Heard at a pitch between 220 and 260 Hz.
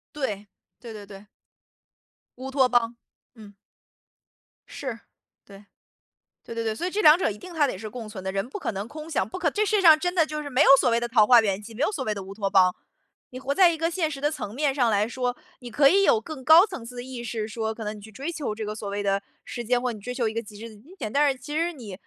Yes: high, 245 Hz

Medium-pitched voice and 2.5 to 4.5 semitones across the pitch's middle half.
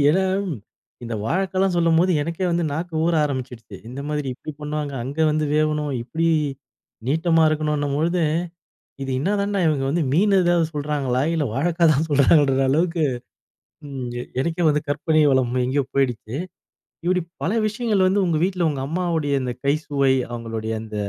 Yes: medium, 155 Hz; average, 3.9 semitones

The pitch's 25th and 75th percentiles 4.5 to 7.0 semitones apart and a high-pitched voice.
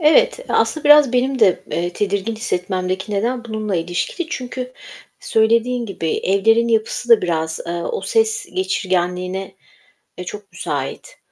Yes: wide, 5.5 semitones; high, 220 Hz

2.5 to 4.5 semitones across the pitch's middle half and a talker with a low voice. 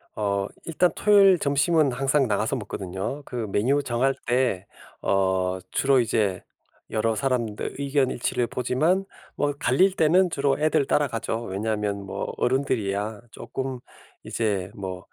No: wide, 5.5 semitones; low, 125 Hz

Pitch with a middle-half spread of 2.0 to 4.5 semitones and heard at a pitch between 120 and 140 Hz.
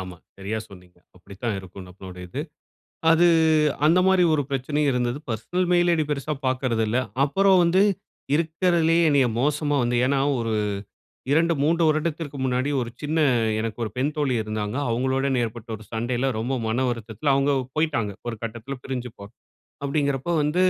No: average, 5.3 semitones; low, 135 Hz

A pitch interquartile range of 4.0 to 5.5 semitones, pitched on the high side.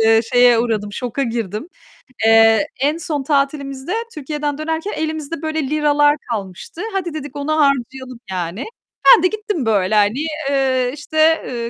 Yes: average, 5.2 semitones; very high, 275 Hz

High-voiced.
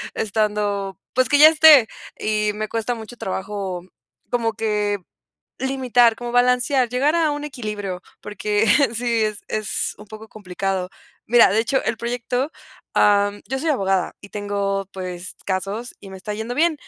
Yes: high, 215 Hz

